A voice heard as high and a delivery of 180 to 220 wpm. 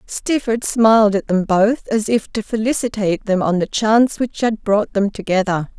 Yes: high, 215 Hz; average, 185 wpm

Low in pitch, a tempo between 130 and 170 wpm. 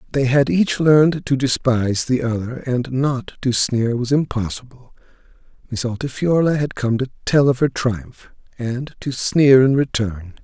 Yes: low, 130 Hz; average, 160 wpm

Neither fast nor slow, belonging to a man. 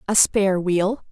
No: average, 160 wpm; female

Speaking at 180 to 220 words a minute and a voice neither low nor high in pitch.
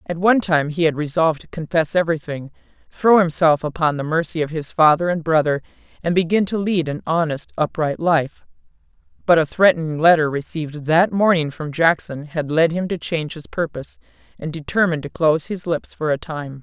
Yes: average, 190 wpm; medium, 160 Hz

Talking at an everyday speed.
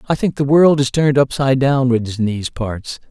No: fast, 215 wpm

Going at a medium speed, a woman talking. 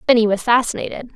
Yes: average, 155 wpm; female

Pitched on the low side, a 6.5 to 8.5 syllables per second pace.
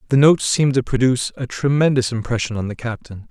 Yes: low, 125 Hz; 6.6 syllables/s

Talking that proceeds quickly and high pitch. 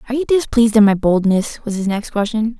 Yes: fast, 230 wpm; high, 220 Hz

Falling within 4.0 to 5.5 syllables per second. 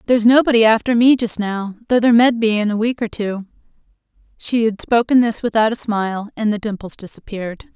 No: 5.9 syllables/s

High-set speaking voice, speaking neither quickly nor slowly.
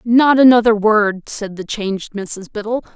Yes: high, 215 Hz; average, 160 wpm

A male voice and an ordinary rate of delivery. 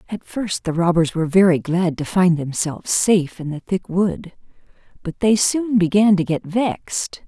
No: female; average, 180 wpm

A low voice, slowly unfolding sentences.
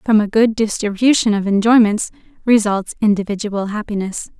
No: high, 215 Hz; slow, 125 wpm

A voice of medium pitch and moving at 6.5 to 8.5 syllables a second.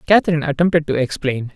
Yes: medium, 155 Hz; 7.1 syllables/s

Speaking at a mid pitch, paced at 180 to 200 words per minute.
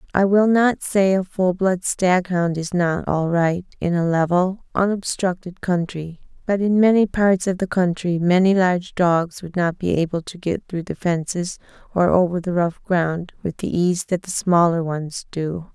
Yes: medium, 180 Hz; average, 190 wpm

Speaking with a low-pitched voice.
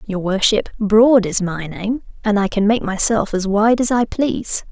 No: high, 210 Hz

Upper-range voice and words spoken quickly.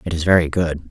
No: very low, 80 Hz; fast, 265 wpm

